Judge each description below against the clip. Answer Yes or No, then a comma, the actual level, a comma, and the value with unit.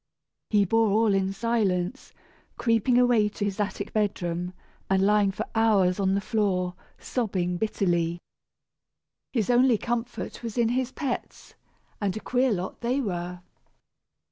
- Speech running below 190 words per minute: Yes, average, 140 wpm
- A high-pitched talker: Yes, high, 210 Hz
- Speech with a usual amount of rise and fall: Yes, average, 3.6 semitones